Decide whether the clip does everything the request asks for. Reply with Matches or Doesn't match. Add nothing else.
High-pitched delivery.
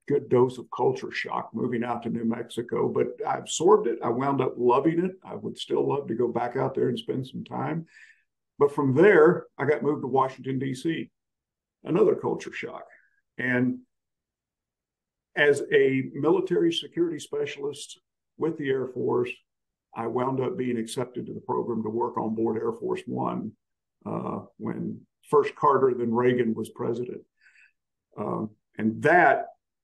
Doesn't match